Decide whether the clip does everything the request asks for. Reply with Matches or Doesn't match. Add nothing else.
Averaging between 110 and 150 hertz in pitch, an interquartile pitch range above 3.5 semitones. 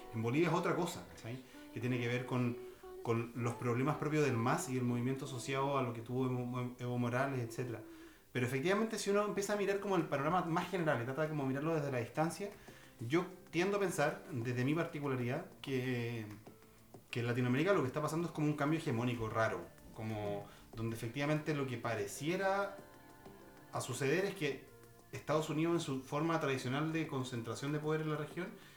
Matches